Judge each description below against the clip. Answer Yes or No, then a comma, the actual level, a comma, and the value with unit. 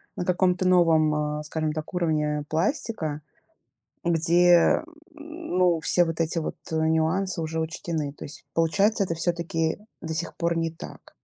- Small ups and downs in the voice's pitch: Yes, narrow, 2.1 semitones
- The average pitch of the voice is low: No, medium, 165 Hz